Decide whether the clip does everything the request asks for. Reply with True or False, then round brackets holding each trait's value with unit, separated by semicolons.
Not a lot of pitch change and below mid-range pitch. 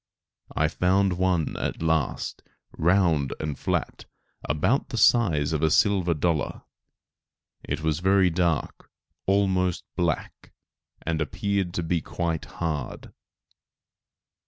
False (3.2 semitones; 85 Hz)